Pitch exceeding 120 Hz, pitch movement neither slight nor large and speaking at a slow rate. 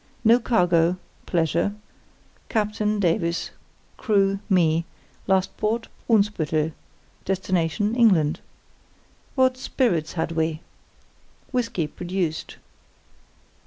Yes: medium, 185 Hz; average, 4.4 semitones; slow, 80 wpm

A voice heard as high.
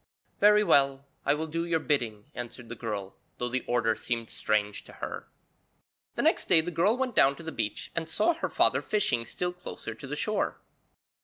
No: medium, 140 Hz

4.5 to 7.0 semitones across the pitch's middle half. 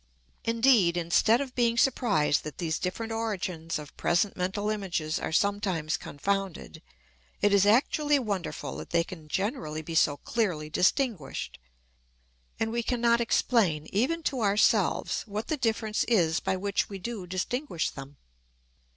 Yes: wide, 5.4 semitones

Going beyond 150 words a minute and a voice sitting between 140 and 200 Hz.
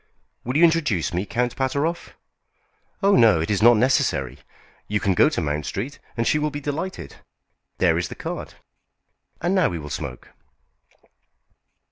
No: average, 160 wpm; low, 120 Hz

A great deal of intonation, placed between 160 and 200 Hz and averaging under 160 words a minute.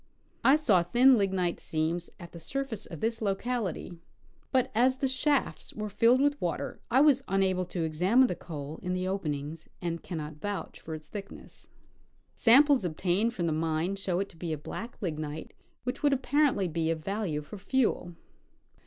No: wide, 6.7 semitones; high, 190 Hz; average, 180 wpm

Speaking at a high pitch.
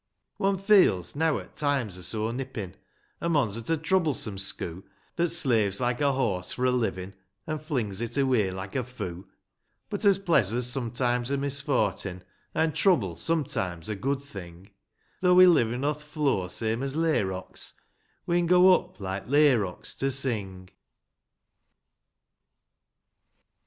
No: low, 125 Hz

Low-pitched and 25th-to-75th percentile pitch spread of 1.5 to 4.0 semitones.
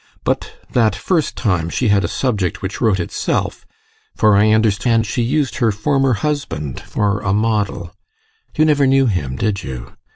No: low, 110 Hz; average, 4.7 semitones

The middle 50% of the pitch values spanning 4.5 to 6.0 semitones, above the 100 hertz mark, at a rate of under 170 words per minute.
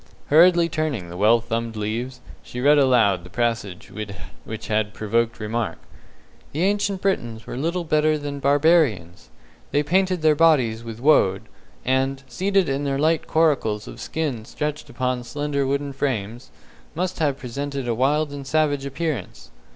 Yes: average, 5.1 semitones; low, 135 Hz; average, 150 wpm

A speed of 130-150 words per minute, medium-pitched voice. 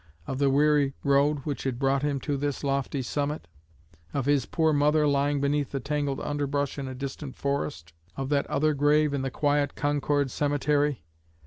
No: average, 180 wpm; medium, 145 Hz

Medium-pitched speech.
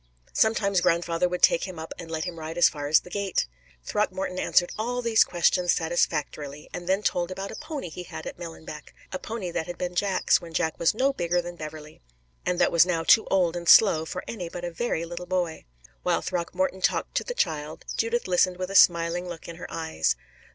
Yes: medium, 175 Hz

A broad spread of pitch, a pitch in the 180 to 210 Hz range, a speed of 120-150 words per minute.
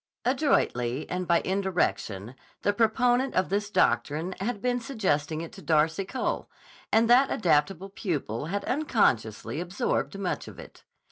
Yes: wide, 6.7 semitones; high, 190 Hz; average, 140 wpm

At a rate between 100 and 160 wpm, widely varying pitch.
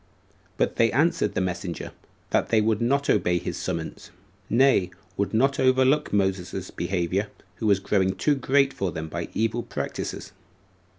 Yes: average, 155 wpm; wide, 5.9 semitones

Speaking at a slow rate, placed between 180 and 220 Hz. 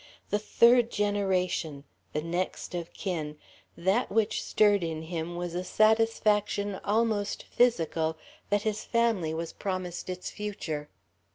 Yes: slow, 125 wpm; high, 190 Hz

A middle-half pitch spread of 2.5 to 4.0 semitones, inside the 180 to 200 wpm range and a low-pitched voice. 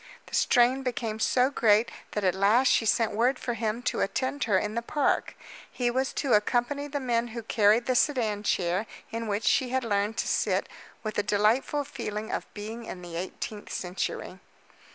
No: average, 3.1 semitones; average, 190 wpm; high, 230 Hz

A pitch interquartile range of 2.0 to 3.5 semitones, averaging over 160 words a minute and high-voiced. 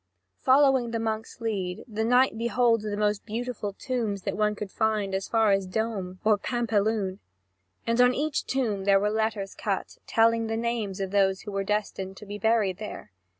Yes: narrow, 2.6 semitones; average, 185 wpm; high, 215 Hz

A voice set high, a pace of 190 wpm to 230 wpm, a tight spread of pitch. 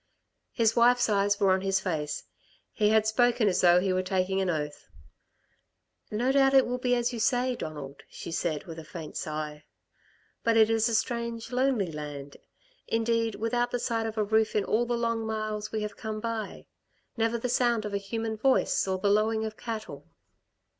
No: high, 220 Hz; average, 195 wpm; average, 3.5 semitones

